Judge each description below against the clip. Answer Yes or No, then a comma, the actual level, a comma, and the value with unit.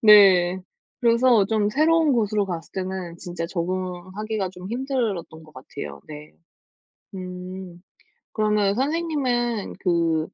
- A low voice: No, high, 190 Hz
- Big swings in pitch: No, average, 4.5 semitones